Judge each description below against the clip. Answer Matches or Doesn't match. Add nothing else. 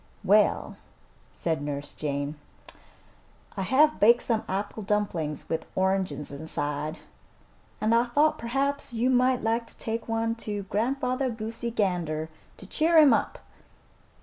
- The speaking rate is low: Matches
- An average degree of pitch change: Doesn't match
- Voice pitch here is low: Doesn't match